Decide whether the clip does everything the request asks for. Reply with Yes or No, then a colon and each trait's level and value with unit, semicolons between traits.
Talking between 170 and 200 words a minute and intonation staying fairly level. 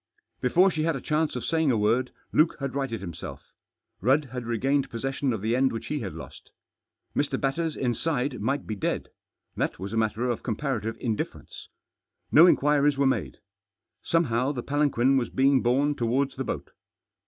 No: average, 175 wpm; average, 3.8 semitones